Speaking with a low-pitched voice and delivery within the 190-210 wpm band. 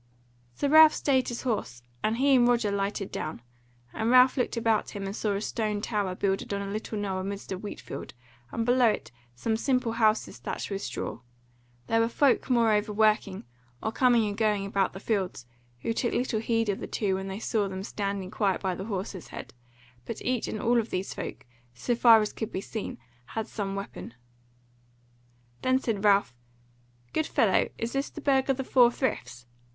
No: high, 215 Hz; average, 195 wpm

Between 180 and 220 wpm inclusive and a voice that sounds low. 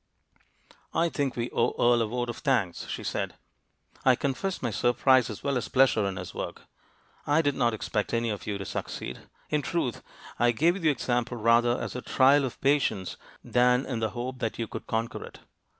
Yes: average, 200 wpm; low, 125 Hz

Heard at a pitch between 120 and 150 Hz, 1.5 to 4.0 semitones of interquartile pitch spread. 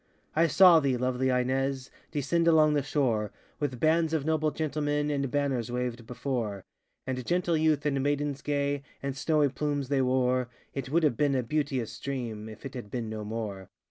Yes: medium, 140 Hz; average, 3.0 semitones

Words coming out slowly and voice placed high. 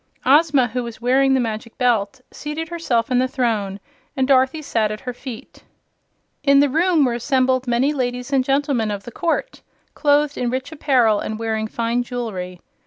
No: average, 175 wpm; very high, 250 Hz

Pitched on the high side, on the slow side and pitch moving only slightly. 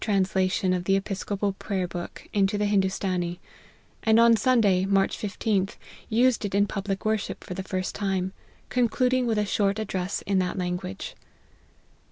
No: high, 195 Hz; average, 160 wpm; narrow, 2.2 semitones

